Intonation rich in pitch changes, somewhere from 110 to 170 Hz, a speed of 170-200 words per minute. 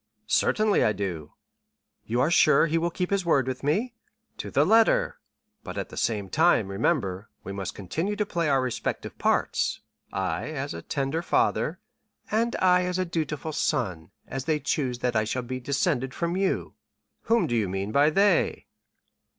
Yes: wide, 7.7 semitones; medium, 140 Hz; average, 175 wpm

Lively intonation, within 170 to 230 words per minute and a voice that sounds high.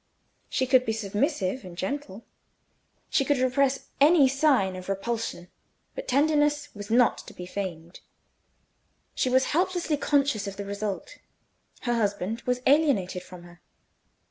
No: wide, 6.3 semitones; average, 140 wpm; high, 240 Hz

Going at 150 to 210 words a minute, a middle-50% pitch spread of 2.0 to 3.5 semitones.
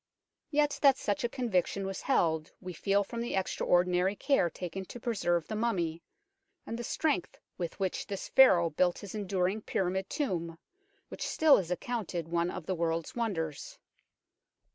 No: average, 160 wpm; average, 4.7 semitones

